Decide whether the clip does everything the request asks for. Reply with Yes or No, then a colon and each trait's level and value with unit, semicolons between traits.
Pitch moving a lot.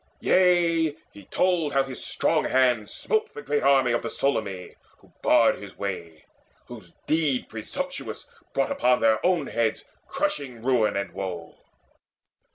Yes: wide, 7.3 semitones